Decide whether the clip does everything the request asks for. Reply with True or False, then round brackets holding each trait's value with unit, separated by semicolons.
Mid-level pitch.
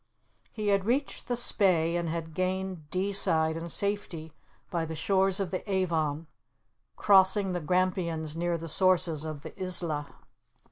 True (175 Hz)